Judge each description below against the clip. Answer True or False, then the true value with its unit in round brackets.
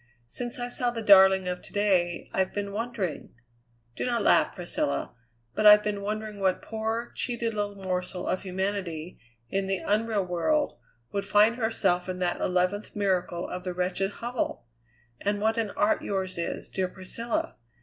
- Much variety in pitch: False (3.1 semitones)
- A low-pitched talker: False (200 Hz)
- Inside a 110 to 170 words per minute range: True (165 wpm)